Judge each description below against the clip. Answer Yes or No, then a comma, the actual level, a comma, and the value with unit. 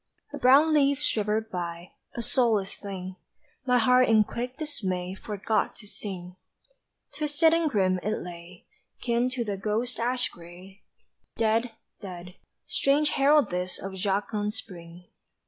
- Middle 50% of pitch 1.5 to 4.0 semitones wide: No, average, 5.3 semitones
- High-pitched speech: Yes, high, 210 Hz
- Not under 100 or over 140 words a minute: Yes, slow, 135 wpm